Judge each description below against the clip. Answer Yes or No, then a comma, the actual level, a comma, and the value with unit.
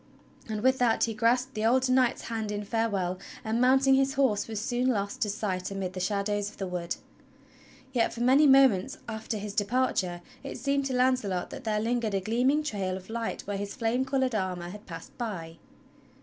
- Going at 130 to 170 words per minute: No, average, 195 wpm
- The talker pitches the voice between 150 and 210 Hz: No, high, 220 Hz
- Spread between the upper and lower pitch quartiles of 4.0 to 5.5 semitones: Yes, average, 4.3 semitones